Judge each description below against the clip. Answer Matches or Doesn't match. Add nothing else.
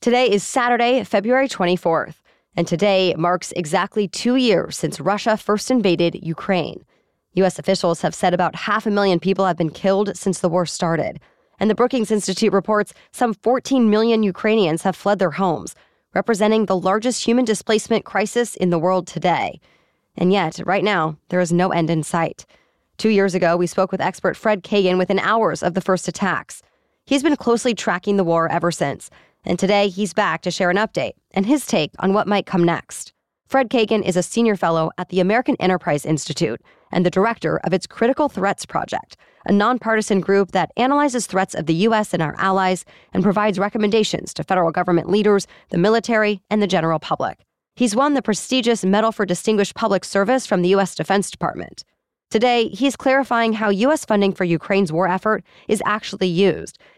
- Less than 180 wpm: Doesn't match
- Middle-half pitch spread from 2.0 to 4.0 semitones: Matches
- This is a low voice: Doesn't match